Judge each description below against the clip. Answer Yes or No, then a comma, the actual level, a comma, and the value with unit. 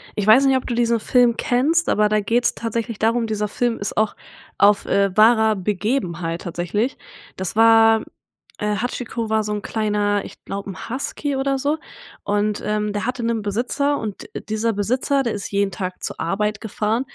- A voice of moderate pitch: No, high, 220 Hz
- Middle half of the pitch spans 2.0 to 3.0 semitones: Yes, average, 2.7 semitones